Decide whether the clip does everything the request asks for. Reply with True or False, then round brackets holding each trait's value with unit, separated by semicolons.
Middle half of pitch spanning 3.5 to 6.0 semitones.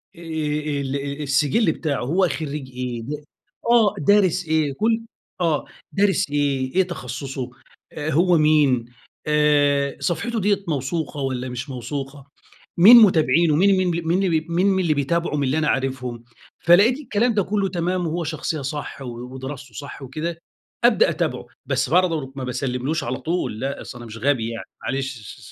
True (4.5 semitones)